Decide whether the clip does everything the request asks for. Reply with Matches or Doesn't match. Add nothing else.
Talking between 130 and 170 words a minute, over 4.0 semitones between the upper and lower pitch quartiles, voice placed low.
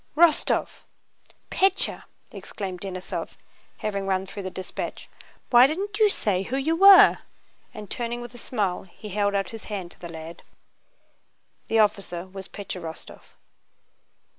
Doesn't match